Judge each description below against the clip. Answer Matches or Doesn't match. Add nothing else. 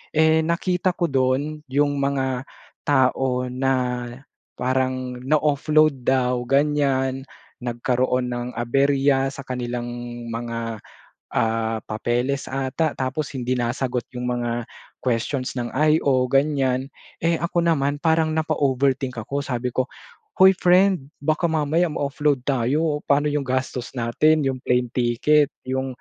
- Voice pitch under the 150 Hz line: Matches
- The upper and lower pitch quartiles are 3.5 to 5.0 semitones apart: Doesn't match